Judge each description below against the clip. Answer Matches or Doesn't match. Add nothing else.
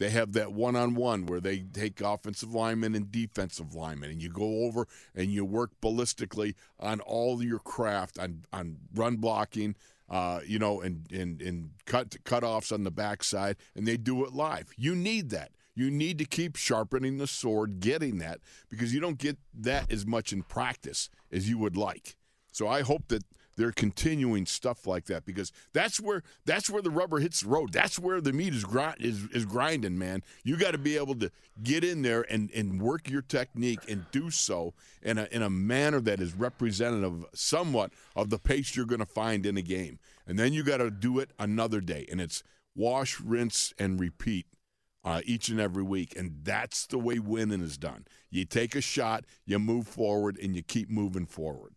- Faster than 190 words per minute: Matches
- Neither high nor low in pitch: Doesn't match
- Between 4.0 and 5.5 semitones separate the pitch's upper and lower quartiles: Matches